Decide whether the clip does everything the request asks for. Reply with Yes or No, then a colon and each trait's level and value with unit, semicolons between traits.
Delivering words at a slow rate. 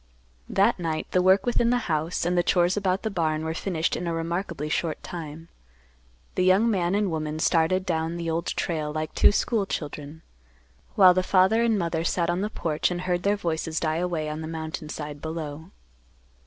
No: average, 195 wpm